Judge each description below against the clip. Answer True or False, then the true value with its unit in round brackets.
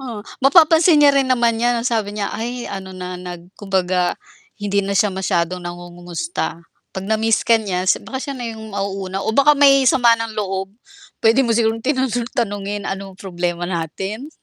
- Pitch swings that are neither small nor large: True (4.3 semitones)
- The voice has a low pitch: False (205 Hz)